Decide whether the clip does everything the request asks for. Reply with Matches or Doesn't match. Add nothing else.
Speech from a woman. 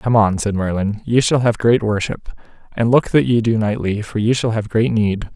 Doesn't match